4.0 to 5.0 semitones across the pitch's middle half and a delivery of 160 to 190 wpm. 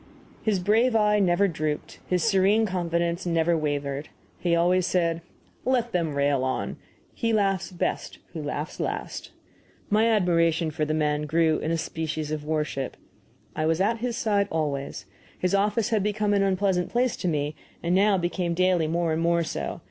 Yes: average, 4.3 semitones; average, 170 wpm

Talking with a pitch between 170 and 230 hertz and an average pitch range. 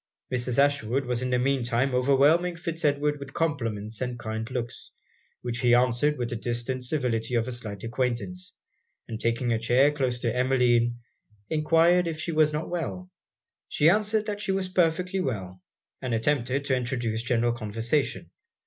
No: low, 125 Hz; average, 4.3 semitones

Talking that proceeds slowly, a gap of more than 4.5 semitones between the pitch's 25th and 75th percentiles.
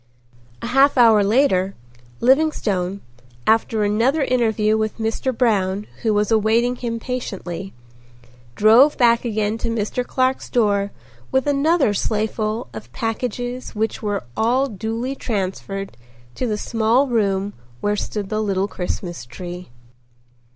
No: slow, 125 wpm; average, 3.4 semitones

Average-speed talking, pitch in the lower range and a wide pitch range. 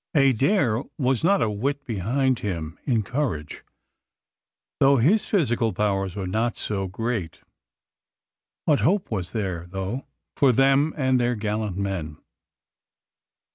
No: slow, 125 wpm; low, 115 Hz; wide, 5.7 semitones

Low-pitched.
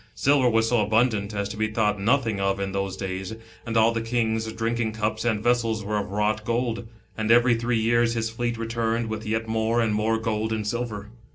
Yes: low, 110 Hz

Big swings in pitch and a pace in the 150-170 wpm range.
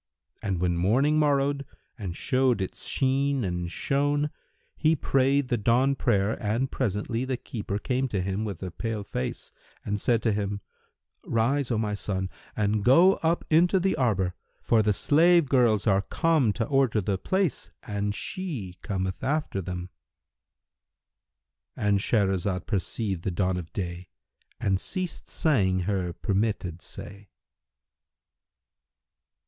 No: wide, 6.0 semitones; slow, 135 wpm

